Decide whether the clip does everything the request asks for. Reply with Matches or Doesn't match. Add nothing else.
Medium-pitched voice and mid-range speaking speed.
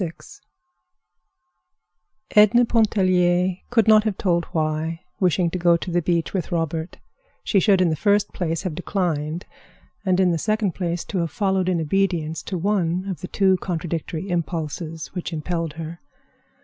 Matches